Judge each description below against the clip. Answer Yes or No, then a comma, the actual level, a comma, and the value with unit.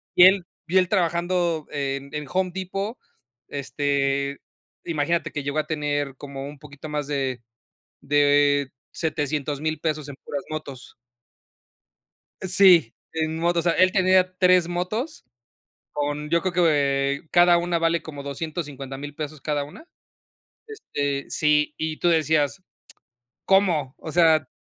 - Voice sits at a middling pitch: Yes, medium, 155 Hz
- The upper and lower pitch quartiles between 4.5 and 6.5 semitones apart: No, average, 3.5 semitones